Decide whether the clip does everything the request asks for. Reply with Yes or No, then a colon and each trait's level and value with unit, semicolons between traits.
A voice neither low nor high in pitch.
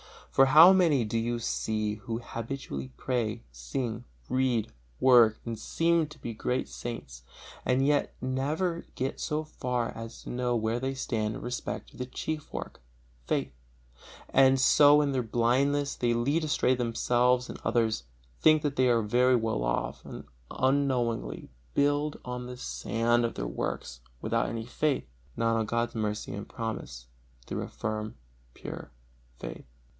No: low, 120 Hz